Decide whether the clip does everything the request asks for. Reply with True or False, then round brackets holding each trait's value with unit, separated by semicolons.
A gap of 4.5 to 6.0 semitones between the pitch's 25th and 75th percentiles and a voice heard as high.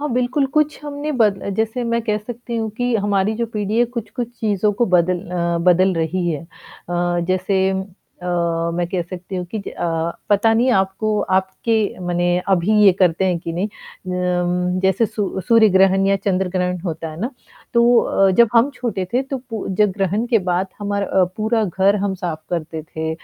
False (3.8 semitones; 195 Hz)